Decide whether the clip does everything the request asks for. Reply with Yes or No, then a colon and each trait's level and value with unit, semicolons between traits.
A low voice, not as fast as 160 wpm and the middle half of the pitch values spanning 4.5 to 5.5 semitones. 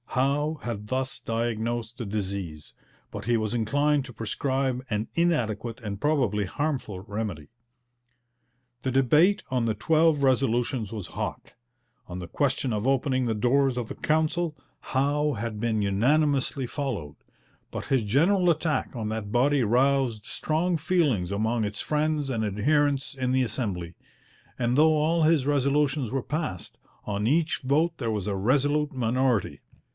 Yes: low, 130 Hz; average, 150 wpm; average, 5.0 semitones